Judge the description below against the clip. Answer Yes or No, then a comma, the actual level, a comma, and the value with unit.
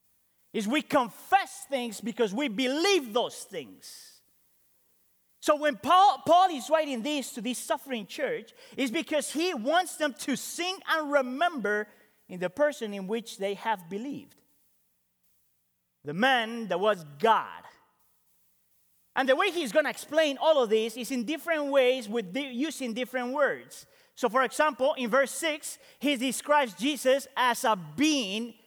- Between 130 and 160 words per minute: Yes, average, 150 wpm